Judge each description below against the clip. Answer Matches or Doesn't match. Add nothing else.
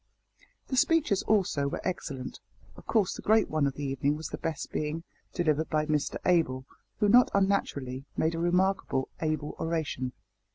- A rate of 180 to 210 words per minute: Doesn't match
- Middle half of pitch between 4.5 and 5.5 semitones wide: Matches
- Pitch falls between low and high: Matches